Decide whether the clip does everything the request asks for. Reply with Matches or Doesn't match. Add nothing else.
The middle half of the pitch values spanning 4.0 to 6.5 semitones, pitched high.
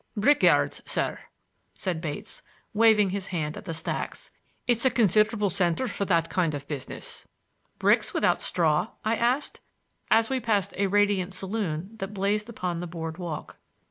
Matches